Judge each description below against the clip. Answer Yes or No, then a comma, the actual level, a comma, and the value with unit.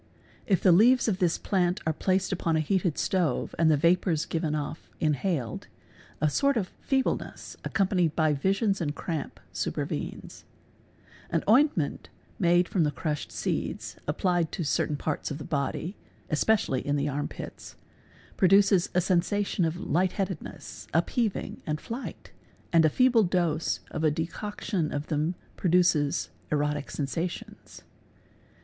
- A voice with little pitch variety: No, average, 4.0 semitones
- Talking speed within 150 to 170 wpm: No, average, 140 wpm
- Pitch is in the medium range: Yes, medium, 170 Hz